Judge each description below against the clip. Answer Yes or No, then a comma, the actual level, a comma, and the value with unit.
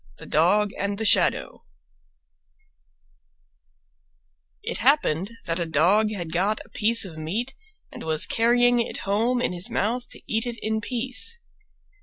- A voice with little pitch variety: No, average, 5.1 semitones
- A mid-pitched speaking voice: No, high, 215 Hz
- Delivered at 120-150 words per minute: Yes, average, 145 wpm